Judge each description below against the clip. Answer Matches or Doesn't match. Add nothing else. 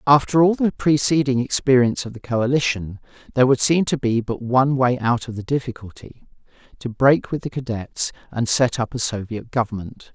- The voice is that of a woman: Doesn't match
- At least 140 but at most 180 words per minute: Matches